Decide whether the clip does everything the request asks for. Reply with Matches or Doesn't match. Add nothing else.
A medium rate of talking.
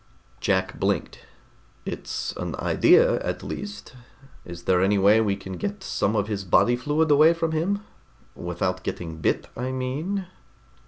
Matches